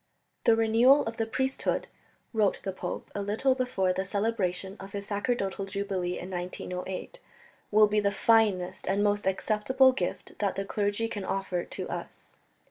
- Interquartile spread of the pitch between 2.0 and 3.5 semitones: Yes, average, 2.7 semitones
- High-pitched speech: Yes, high, 205 Hz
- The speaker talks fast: No, average, 160 wpm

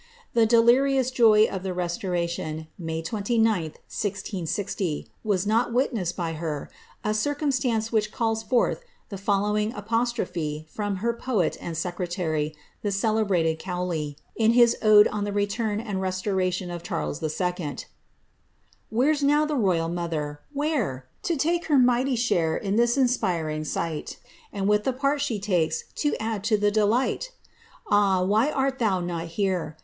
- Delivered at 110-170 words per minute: Yes, average, 155 wpm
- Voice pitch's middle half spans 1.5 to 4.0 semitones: No, average, 5.2 semitones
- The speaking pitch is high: Yes, high, 205 Hz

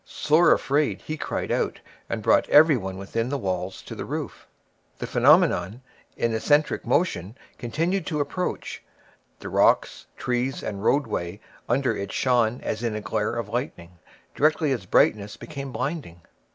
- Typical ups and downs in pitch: No, wide, 6.3 semitones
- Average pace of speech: Yes, average, 150 wpm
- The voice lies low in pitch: Yes, low, 120 Hz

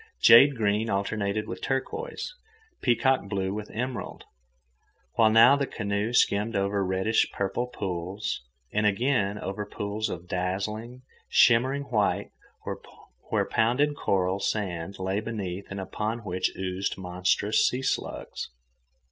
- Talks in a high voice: No, low, 105 Hz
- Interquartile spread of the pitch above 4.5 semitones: No, average, 3.3 semitones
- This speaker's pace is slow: Yes, slow, 120 wpm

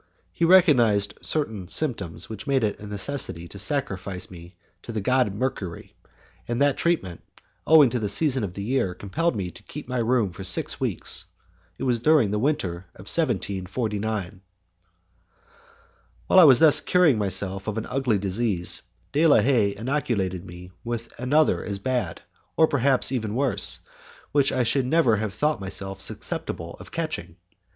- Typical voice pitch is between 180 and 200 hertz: No, low, 110 Hz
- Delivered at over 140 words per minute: Yes, average, 160 wpm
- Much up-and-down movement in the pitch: Yes, wide, 5.8 semitones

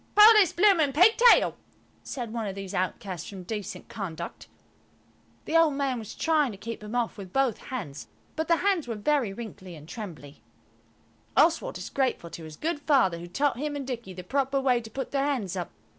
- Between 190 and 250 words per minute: Yes, average, 195 wpm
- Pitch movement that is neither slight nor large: No, wide, 7.1 semitones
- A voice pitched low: No, high, 240 Hz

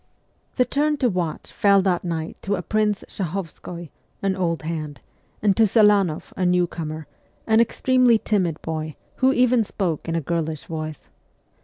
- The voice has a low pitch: No, medium, 180 Hz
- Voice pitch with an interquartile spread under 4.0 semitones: No, average, 4.9 semitones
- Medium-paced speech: Yes, average, 160 wpm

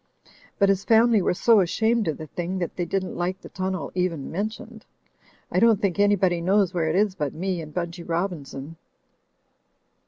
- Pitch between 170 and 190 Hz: Yes, medium, 185 Hz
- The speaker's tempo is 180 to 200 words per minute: Yes, average, 185 wpm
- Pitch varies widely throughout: No, average, 3.1 semitones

